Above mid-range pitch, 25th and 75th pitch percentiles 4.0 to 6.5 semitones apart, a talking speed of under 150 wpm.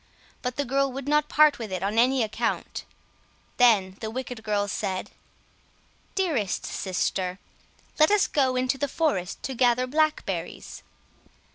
Yes: very high, 250 Hz; average, 5.3 semitones; average, 140 wpm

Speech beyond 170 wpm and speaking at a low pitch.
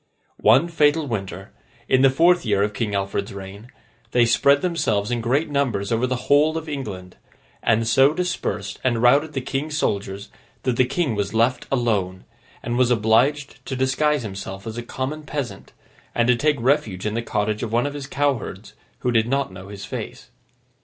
Yes: average, 185 wpm; low, 120 Hz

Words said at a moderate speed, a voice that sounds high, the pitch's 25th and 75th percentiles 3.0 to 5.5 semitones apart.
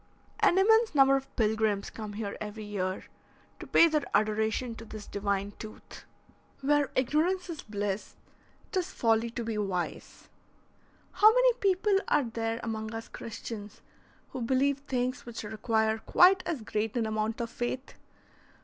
Yes: average, 150 wpm; high, 230 Hz; average, 4.7 semitones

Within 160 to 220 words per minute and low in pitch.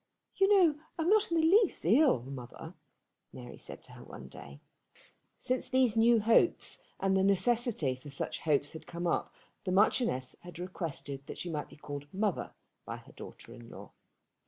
No: average, 175 wpm; high, 190 Hz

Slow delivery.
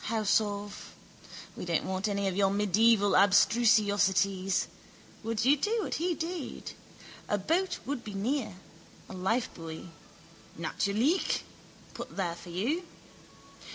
Yes: slow, 120 wpm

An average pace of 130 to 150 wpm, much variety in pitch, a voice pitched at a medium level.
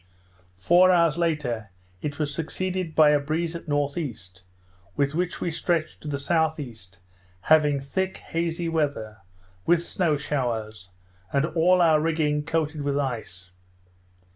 No: slow, 135 wpm; average, 2.9 semitones; medium, 155 Hz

